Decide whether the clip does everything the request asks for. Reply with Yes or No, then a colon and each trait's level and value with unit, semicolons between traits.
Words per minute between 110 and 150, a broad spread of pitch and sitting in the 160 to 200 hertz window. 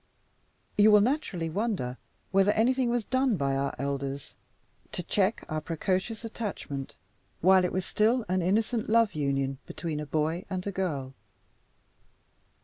Yes: average, 140 wpm; wide, 6.5 semitones; medium, 185 Hz